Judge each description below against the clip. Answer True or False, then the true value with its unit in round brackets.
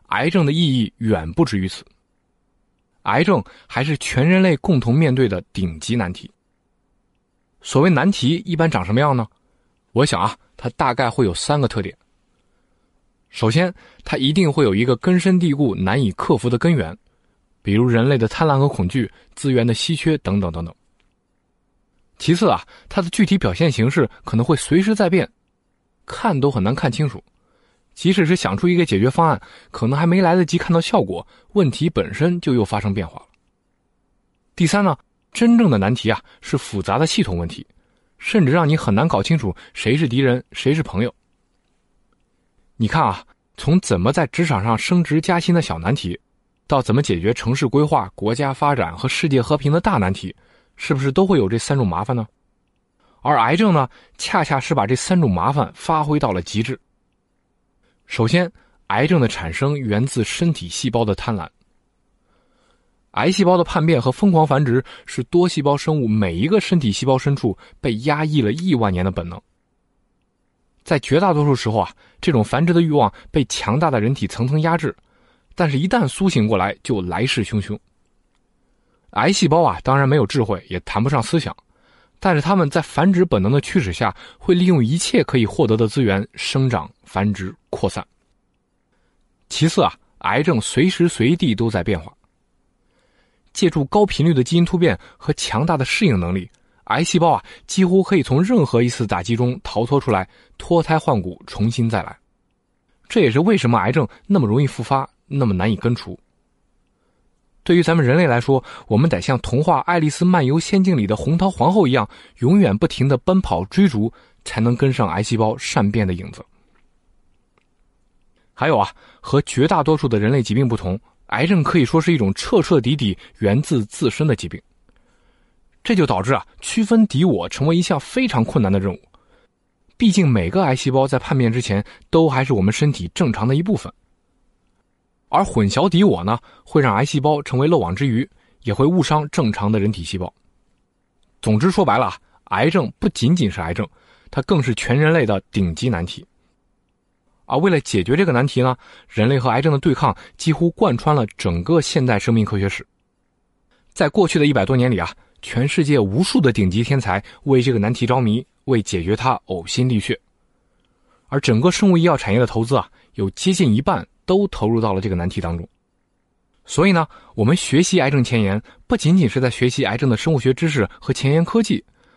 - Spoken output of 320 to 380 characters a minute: False (270 characters per minute)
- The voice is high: False (135 Hz)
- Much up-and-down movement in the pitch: True (7.2 semitones)